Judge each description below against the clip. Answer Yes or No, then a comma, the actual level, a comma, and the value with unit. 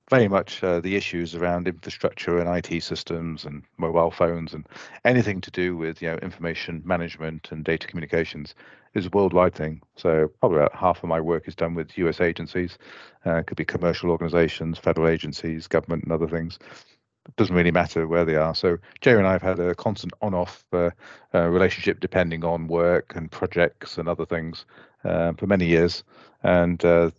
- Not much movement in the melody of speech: Yes, narrow, 1.4 semitones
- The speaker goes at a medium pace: Yes, average, 190 wpm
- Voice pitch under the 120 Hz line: Yes, very low, 85 Hz